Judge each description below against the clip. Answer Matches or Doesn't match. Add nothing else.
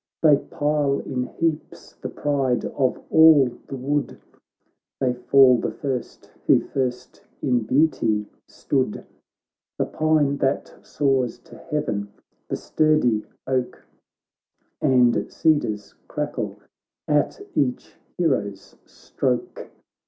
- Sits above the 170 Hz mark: Doesn't match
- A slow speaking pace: Matches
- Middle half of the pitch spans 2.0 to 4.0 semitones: Matches